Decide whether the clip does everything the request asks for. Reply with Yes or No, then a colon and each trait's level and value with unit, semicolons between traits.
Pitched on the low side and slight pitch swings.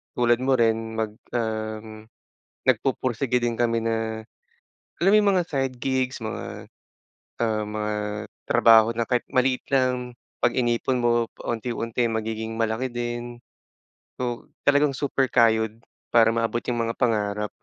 Yes: low, 120 Hz; narrow, 2.2 semitones